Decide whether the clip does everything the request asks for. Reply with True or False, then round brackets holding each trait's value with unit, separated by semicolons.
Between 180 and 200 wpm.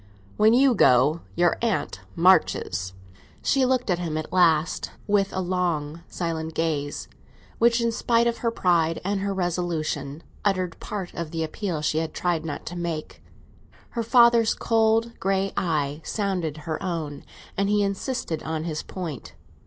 False (155 wpm)